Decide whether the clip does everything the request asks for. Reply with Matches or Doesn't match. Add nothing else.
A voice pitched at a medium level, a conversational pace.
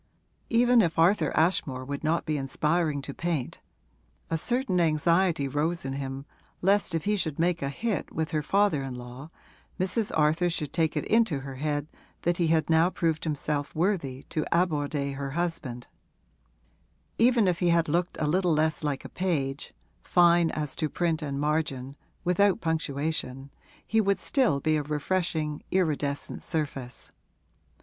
Matches